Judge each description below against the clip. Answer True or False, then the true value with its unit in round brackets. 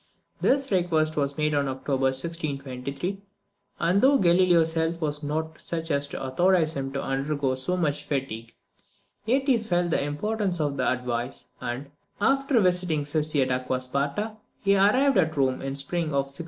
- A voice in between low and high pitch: True (155 Hz)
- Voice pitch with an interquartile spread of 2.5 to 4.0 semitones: False (4.7 semitones)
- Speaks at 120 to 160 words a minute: False (170 wpm)